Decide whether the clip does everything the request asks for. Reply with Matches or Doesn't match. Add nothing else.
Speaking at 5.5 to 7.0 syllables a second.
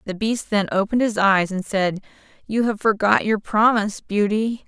Doesn't match